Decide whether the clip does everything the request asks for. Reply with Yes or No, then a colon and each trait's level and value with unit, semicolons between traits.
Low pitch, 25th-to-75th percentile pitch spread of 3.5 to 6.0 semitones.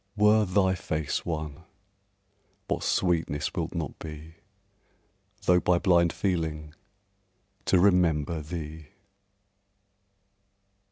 No: very low, 85 Hz; average, 2.8 semitones